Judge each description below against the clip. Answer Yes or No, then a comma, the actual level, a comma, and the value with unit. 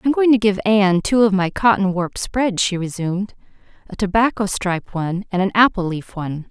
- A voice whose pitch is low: No, high, 200 Hz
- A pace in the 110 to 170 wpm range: No, fast, 205 wpm